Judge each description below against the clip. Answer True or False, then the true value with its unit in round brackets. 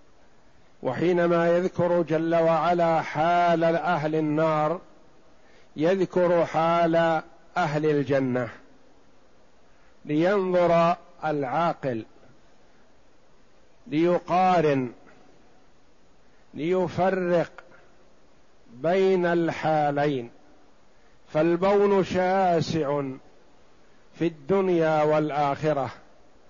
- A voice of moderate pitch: True (165 Hz)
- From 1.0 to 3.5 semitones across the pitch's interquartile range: True (2.4 semitones)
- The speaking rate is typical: False (50 wpm)